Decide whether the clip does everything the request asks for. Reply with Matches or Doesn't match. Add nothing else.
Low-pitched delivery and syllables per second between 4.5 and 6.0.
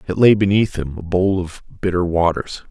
Matches